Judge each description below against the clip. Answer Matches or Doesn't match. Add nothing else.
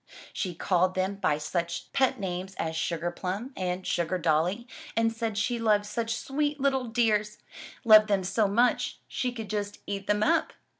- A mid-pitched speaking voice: Doesn't match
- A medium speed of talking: Matches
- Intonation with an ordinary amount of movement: Matches